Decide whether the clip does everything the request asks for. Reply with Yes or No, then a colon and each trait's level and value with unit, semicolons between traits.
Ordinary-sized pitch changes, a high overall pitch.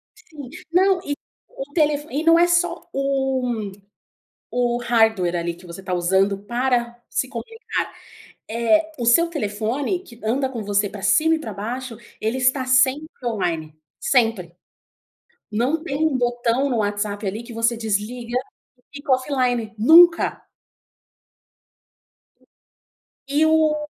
Yes: average, 5.0 semitones; high, 245 Hz